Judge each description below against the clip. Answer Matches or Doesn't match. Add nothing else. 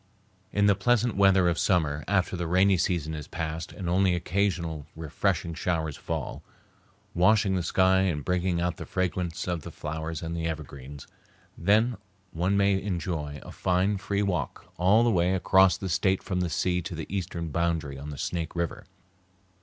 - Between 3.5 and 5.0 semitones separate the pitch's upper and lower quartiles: Doesn't match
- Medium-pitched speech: Doesn't match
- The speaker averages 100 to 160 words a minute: Doesn't match